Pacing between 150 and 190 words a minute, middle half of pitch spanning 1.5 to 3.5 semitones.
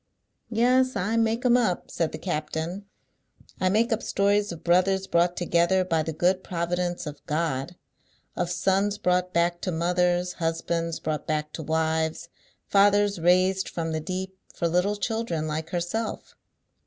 Yes: average, 155 wpm; average, 3.2 semitones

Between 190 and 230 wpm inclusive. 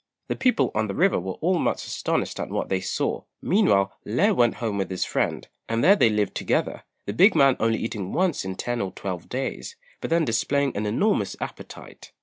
Yes: fast, 205 wpm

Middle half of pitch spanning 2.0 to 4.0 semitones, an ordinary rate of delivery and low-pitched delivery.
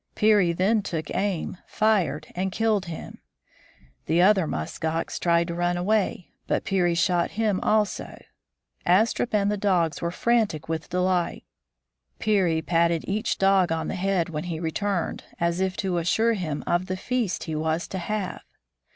No: average, 3.2 semitones; average, 160 wpm; medium, 180 Hz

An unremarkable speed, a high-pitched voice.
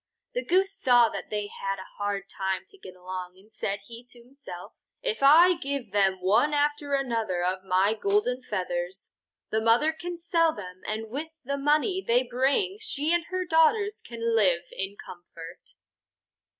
Yes: average, 175 wpm; high, 235 Hz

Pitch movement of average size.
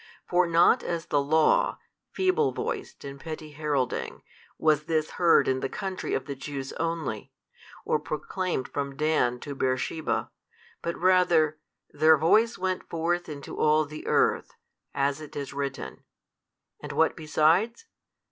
Yes: average, 3.3 semitones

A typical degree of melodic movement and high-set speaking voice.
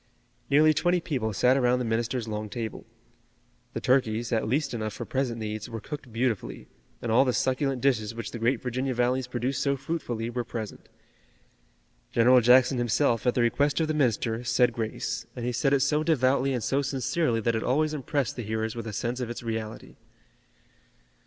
No: average, 3.0 semitones; low, 125 Hz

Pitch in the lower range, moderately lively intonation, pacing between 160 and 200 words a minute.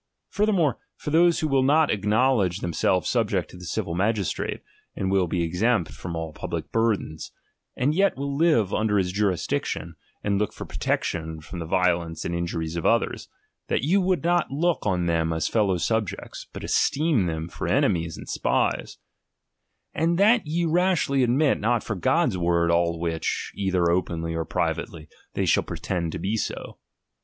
No: very low, 95 Hz; wide, 8.5 semitones; average, 170 wpm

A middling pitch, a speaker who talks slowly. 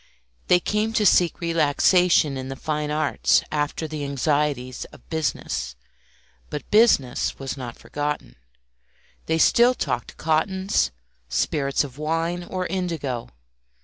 Yes: medium, 155 Hz; slow, 120 wpm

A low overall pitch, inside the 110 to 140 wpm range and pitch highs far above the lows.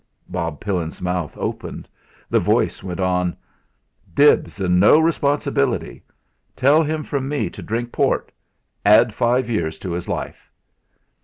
Yes: low, 105 Hz; slow, 135 wpm; wide, 7.5 semitones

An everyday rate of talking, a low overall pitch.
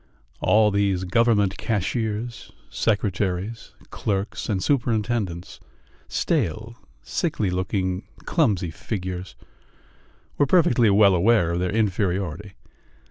No: slow, 90 wpm; low, 100 Hz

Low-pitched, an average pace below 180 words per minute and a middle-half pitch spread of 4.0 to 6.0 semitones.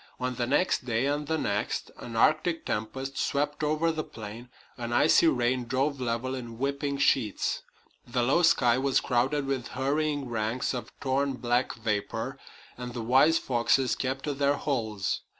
No: low, 130 Hz; average, 165 wpm; average, 3.1 semitones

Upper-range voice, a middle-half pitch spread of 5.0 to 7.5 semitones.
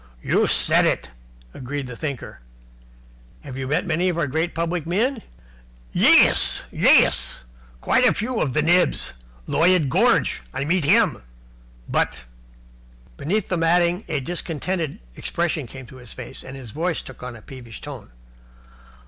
No: medium, 155 Hz; average, 5.3 semitones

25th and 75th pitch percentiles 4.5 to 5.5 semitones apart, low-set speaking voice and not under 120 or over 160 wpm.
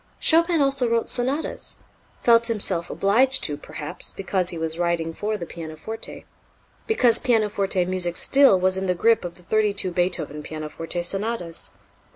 No: average, 5.1 semitones; high, 190 Hz; average, 155 wpm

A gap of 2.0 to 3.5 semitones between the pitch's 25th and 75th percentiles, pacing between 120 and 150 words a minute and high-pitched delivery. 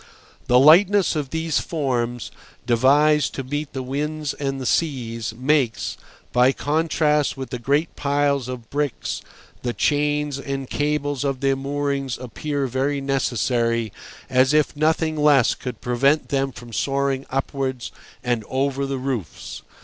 No: narrow, 2.4 semitones; average, 140 wpm; low, 135 Hz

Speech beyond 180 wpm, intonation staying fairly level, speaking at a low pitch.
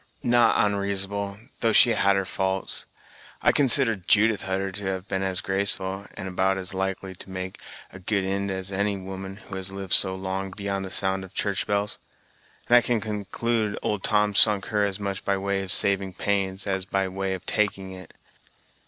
Yes: average, 190 wpm; narrow, 1.2 semitones; very low, 95 Hz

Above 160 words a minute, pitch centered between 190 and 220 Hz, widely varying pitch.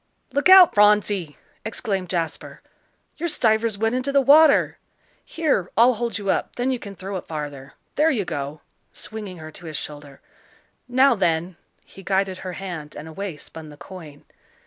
Yes: average, 170 wpm; high, 195 Hz; wide, 6.8 semitones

